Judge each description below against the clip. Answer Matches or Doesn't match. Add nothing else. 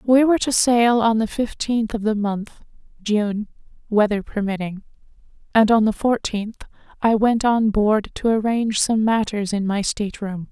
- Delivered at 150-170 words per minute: Matches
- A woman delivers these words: Matches